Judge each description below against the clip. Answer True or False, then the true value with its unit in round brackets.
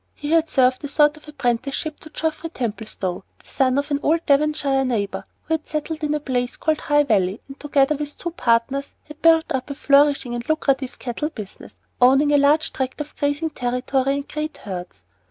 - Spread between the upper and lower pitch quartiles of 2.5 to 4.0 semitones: True (3.2 semitones)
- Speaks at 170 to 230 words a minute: True (195 wpm)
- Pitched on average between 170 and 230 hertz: False (280 Hz)